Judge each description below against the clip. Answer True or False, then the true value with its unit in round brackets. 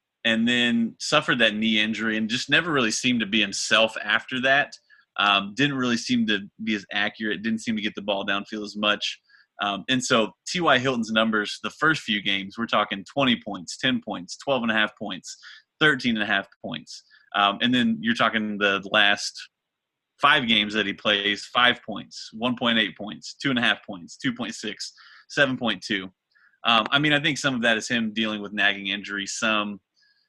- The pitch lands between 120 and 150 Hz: False (110 Hz)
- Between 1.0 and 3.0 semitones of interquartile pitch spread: True (2.4 semitones)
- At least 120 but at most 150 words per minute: False (190 wpm)